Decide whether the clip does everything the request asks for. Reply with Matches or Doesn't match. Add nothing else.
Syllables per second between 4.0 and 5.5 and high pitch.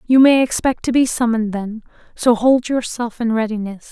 Matches